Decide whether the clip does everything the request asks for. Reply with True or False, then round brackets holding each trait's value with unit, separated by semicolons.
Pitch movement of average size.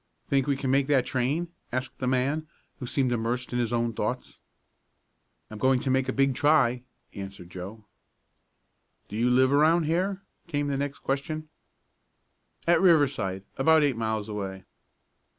True (3.8 semitones)